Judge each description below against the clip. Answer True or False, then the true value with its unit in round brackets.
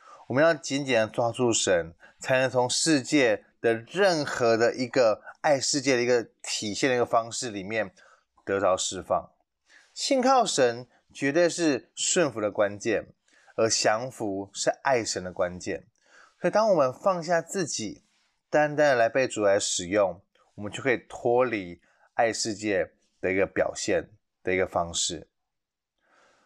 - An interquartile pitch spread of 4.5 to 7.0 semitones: True (5.5 semitones)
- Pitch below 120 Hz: False (125 Hz)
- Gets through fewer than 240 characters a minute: True (220 characters per minute)